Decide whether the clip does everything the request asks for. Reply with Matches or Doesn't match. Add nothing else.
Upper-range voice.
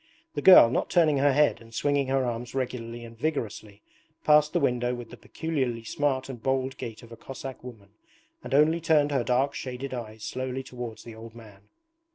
Doesn't match